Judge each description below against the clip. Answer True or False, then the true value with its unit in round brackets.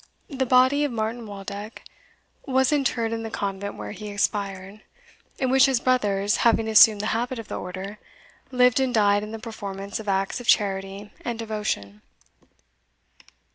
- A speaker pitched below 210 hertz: False (215 Hz)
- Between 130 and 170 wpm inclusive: True (160 wpm)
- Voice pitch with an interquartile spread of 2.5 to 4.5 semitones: True (3.4 semitones)